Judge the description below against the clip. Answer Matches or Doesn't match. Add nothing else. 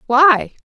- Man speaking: Doesn't match